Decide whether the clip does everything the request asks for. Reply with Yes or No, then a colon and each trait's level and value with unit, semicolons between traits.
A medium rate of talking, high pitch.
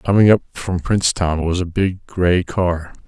No: average, 175 wpm; very low, 90 Hz